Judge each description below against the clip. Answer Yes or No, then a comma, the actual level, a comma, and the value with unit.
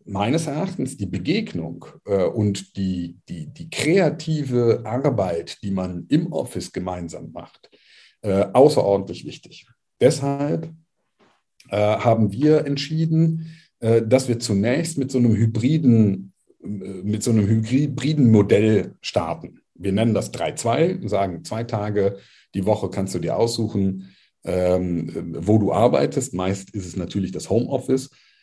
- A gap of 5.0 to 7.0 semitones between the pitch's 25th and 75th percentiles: Yes, wide, 5.6 semitones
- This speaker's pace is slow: No, average, 135 wpm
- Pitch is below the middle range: Yes, low, 110 Hz